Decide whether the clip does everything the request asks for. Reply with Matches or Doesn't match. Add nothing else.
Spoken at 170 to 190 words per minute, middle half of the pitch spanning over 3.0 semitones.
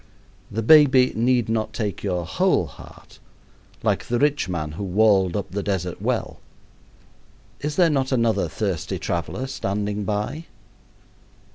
Doesn't match